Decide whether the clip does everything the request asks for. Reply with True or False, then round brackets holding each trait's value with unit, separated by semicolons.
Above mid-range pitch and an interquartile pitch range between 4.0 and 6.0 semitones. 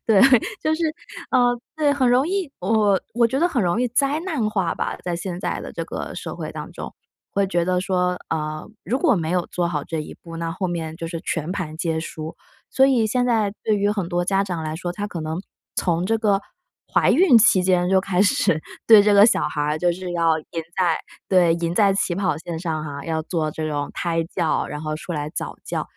False (180 Hz; 4.4 semitones)